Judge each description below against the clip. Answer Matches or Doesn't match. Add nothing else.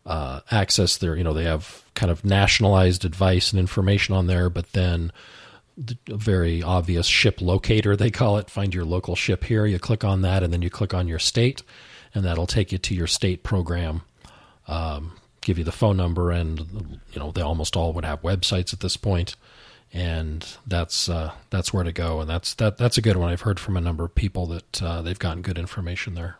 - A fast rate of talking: Matches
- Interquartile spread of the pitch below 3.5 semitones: Matches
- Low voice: Matches